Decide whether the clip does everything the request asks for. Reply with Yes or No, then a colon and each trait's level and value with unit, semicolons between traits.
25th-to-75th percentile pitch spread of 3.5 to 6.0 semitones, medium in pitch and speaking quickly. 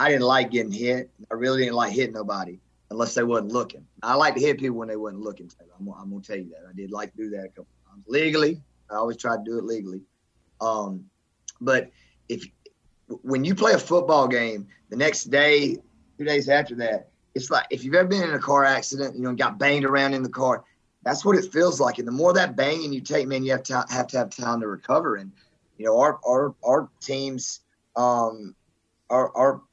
No: average, 4.6 semitones; low, 125 Hz; fast, 235 wpm